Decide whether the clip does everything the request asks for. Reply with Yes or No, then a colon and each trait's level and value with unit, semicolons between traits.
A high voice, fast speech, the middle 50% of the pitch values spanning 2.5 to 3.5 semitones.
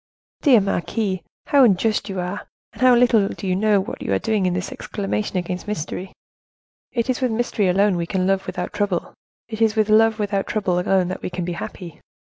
Yes: high, 200 Hz; fast, 210 wpm; average, 3.2 semitones